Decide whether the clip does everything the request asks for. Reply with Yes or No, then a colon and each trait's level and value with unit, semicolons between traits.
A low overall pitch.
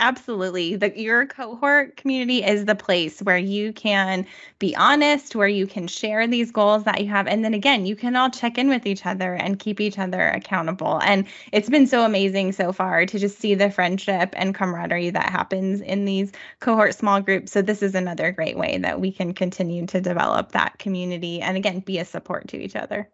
No: high, 200 Hz